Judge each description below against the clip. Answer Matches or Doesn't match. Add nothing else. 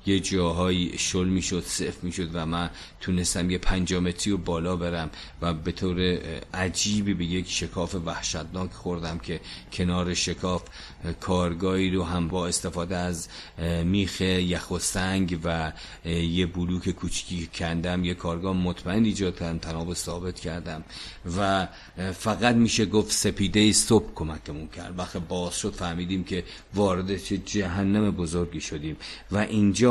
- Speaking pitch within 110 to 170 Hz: Doesn't match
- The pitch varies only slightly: Matches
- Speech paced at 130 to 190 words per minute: Matches